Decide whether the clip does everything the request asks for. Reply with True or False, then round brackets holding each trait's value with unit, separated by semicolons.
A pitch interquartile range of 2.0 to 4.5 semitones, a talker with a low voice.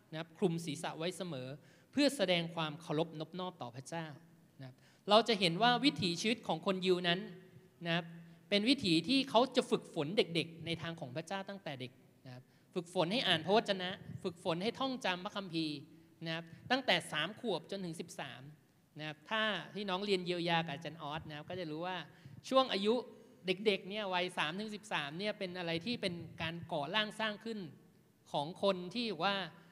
False (3.8 semitones; 180 Hz)